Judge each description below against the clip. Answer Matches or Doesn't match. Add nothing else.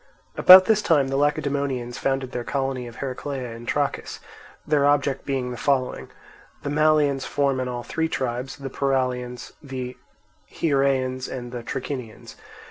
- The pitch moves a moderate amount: Doesn't match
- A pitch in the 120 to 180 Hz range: Matches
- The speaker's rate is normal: Matches